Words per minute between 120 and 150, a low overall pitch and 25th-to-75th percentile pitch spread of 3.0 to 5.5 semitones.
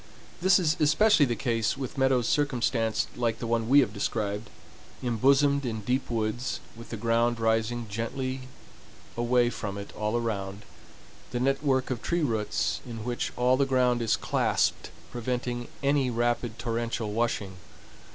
No: average, 145 wpm; low, 120 Hz; narrow, 2.6 semitones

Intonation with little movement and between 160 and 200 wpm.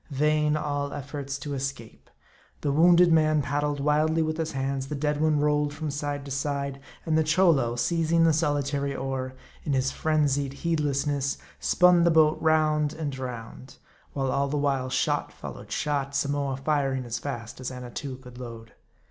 Yes: narrow, 2.2 semitones; average, 165 wpm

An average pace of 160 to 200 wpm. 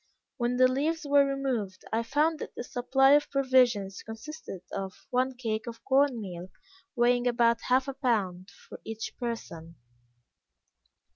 No: average, 145 wpm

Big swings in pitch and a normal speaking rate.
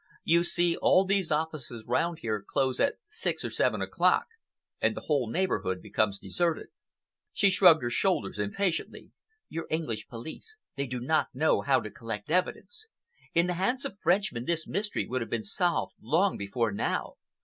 Yes: wide, 7.6 semitones; average, 170 wpm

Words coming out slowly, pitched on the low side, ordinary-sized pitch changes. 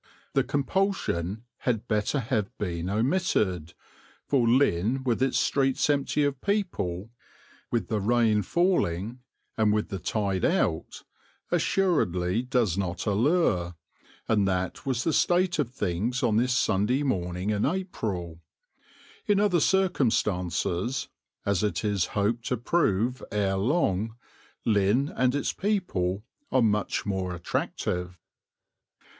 No: slow, 125 wpm; low, 110 Hz; wide, 5.9 semitones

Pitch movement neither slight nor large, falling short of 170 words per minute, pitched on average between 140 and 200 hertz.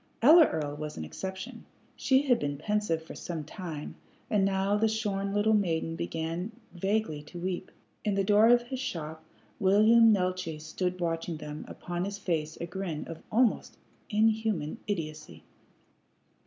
Yes: average, 4.8 semitones; average, 155 wpm; medium, 185 Hz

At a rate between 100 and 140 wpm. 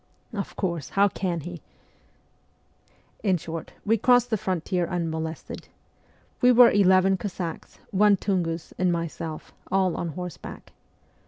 Yes: slow, 135 wpm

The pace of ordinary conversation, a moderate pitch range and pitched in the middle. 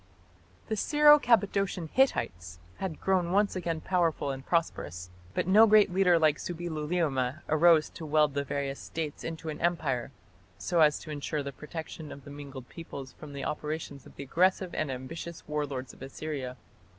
Yes: average, 170 wpm; average, 3.9 semitones; medium, 155 Hz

